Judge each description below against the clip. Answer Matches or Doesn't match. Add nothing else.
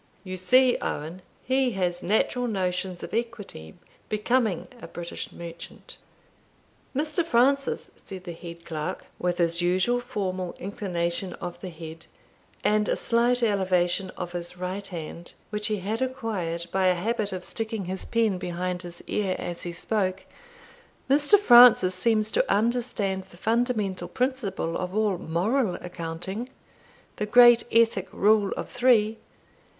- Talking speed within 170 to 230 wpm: Doesn't match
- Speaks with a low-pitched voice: Doesn't match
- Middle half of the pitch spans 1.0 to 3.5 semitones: Doesn't match